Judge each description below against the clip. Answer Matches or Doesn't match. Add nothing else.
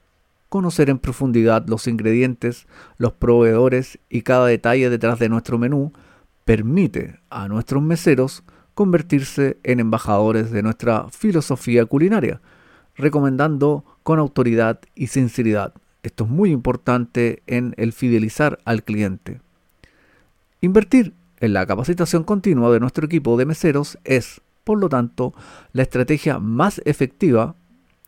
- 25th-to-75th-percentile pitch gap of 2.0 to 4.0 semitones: Doesn't match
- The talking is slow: Matches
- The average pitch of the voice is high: Doesn't match